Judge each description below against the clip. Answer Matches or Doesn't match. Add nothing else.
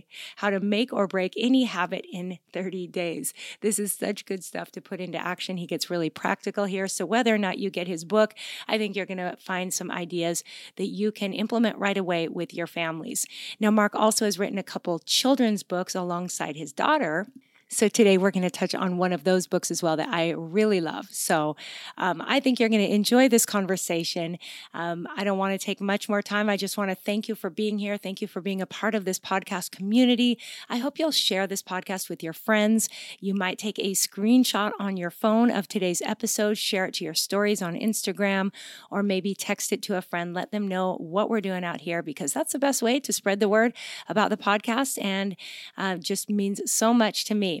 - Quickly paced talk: Matches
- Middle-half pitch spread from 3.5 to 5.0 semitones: Doesn't match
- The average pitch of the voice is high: Matches